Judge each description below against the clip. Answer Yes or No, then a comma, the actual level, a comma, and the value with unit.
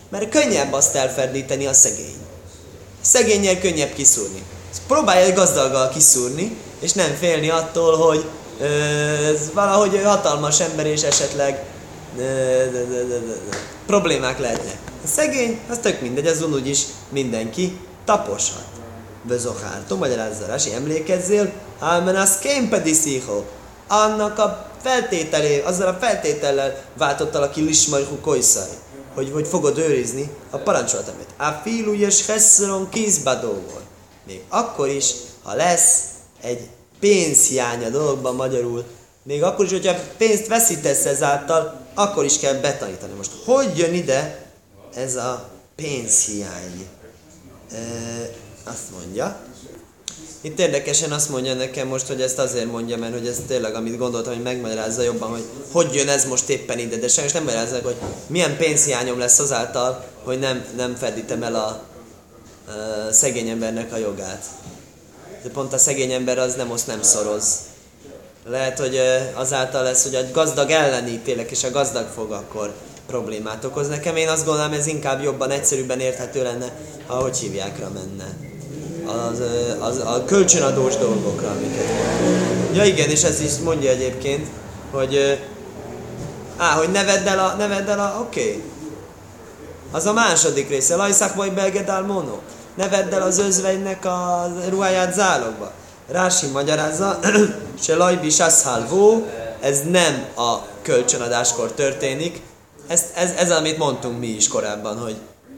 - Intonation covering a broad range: Yes, wide, 6.3 semitones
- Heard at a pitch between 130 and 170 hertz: Yes, medium, 140 Hz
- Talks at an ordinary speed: Yes, average, 135 wpm